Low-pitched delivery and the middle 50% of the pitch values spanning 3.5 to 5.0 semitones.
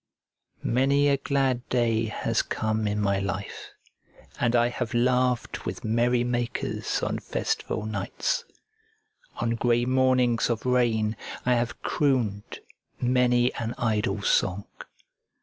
No: low, 120 Hz; narrow, 2.4 semitones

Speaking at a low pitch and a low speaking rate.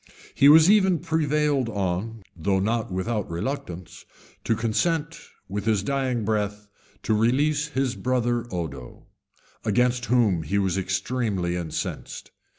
Yes: low, 115 Hz; slow, 125 wpm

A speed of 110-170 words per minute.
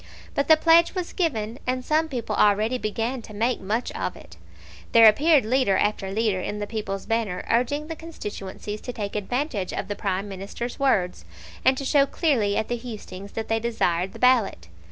No: average, 190 wpm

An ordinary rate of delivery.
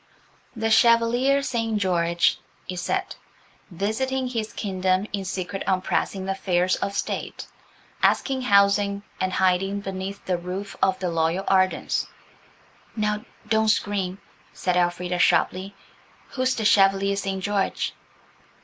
No: slow, 120 wpm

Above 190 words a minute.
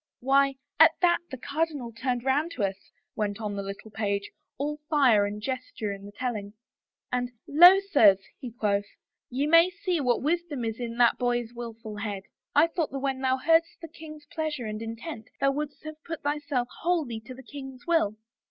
Yes: average, 200 wpm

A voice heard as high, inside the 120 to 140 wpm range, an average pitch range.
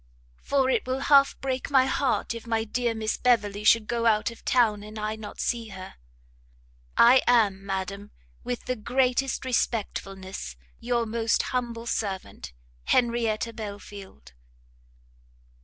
Yes: high, 230 Hz; slow, 135 wpm; average, 3.0 semitones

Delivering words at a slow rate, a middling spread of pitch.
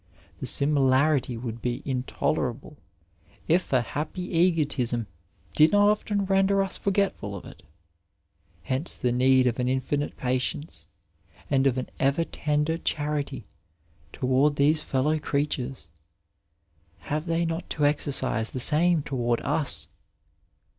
Yes: slow, 125 wpm; average, 3.8 semitones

